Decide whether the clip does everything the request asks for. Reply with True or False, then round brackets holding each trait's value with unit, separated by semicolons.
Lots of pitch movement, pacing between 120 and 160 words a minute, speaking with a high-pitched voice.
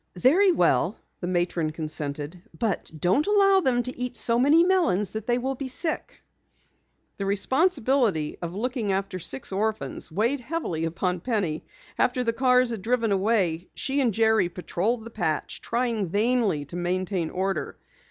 True (6.0 semitones; 155 wpm; 220 Hz)